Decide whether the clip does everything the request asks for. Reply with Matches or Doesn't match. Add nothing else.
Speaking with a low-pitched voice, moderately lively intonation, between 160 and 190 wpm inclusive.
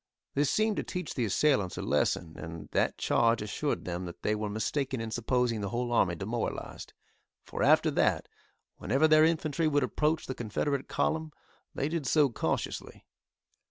Doesn't match